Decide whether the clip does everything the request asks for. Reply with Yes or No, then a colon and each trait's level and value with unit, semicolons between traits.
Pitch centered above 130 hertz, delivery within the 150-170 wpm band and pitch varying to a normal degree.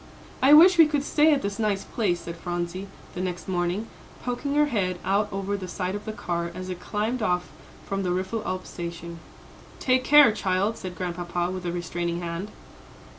No: medium, 185 Hz; average, 185 wpm; average, 3.8 semitones